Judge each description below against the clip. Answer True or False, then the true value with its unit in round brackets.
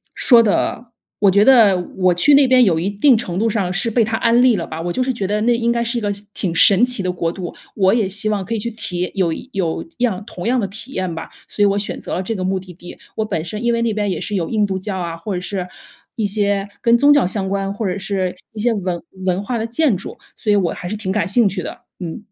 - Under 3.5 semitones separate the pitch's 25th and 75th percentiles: False (3.8 semitones)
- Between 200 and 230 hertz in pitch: True (205 Hz)